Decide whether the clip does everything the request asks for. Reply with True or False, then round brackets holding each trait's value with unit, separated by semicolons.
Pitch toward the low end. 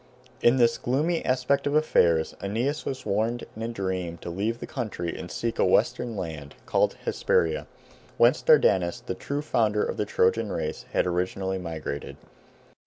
True (105 Hz)